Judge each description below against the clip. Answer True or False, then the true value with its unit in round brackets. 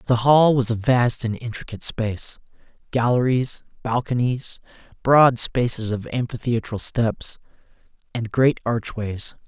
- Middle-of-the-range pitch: False (120 Hz)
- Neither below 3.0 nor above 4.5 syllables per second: True (4.2 syllables/s)